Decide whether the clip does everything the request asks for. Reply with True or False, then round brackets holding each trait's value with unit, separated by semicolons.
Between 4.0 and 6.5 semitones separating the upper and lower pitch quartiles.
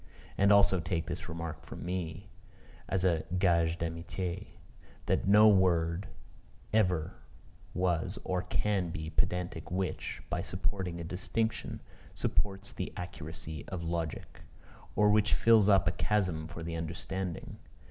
False (2.7 semitones)